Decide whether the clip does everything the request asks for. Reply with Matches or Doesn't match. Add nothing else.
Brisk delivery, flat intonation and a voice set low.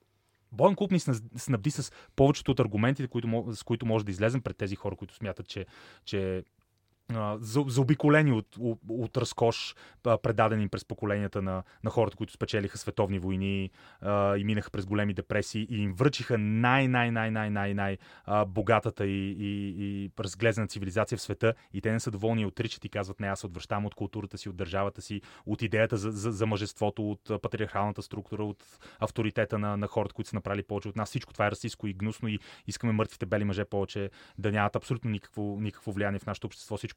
Matches